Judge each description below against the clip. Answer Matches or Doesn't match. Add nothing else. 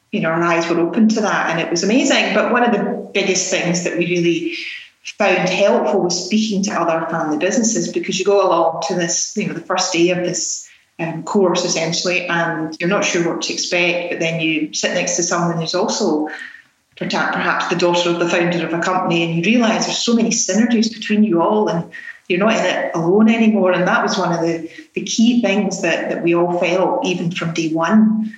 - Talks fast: Matches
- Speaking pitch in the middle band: Matches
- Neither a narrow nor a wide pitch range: Matches